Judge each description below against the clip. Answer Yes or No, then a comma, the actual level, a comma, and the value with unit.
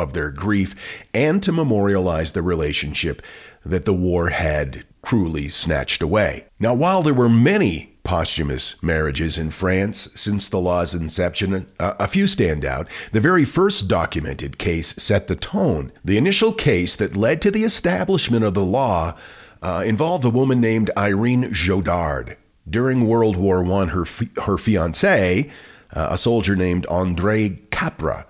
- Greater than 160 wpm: No, average, 155 wpm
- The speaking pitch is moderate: No, very low, 95 Hz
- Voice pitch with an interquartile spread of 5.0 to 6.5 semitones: Yes, average, 5.3 semitones